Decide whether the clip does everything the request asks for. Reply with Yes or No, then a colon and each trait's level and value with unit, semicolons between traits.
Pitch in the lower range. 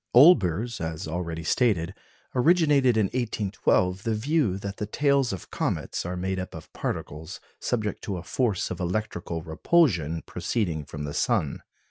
Yes: very low, 95 Hz